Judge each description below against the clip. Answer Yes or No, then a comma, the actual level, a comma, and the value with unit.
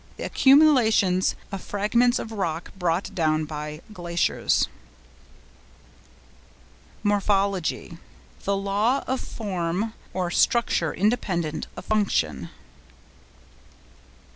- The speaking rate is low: Yes, slow, 80 wpm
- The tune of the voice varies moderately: Yes, average, 4.2 semitones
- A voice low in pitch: No, high, 195 Hz